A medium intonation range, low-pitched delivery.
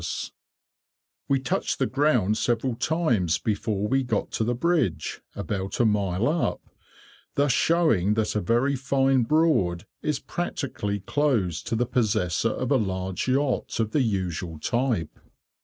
No: wide, 5.7 semitones; low, 115 Hz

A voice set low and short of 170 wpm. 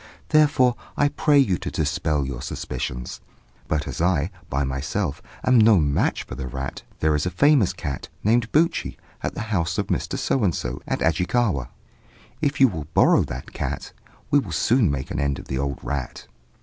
No: very low, 85 Hz; average, 190 wpm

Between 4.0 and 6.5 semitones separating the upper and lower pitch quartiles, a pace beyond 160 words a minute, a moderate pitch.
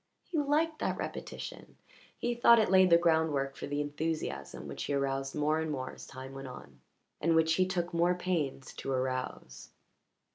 Yes: average, 4.7 semitones; average, 180 wpm; medium, 160 Hz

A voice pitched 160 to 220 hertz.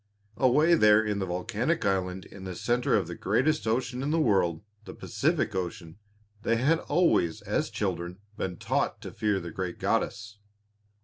No: low, 105 Hz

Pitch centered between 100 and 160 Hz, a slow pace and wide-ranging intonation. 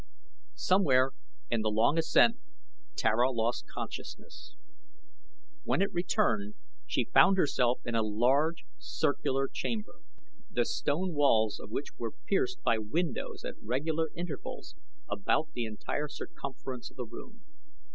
Yes: medium, 140 Hz; slow, 125 wpm; wide, 6.8 semitones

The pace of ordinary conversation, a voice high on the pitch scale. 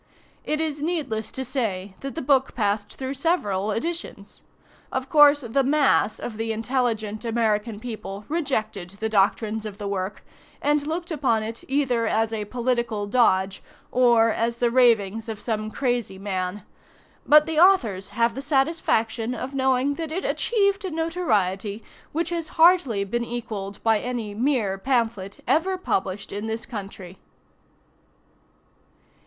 Yes: average, 145 wpm; high, 235 Hz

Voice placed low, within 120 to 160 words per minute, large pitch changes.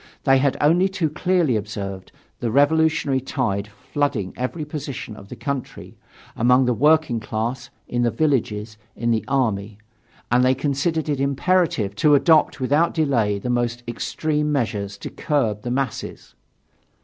No: low, 130 Hz; average, 150 wpm; average, 4.9 semitones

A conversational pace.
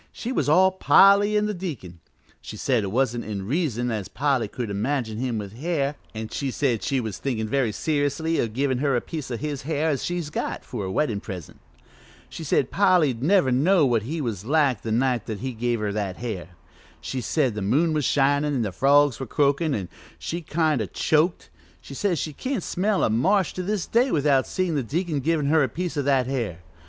No: fast, 215 wpm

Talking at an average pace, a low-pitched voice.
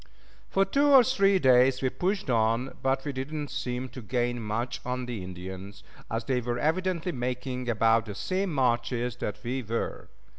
Yes: average, 180 wpm; low, 125 Hz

